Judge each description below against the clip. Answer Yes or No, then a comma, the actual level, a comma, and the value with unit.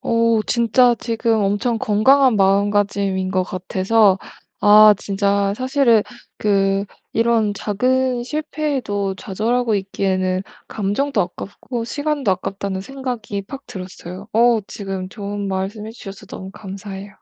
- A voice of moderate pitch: No, high, 205 Hz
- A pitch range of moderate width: Yes, average, 3.3 semitones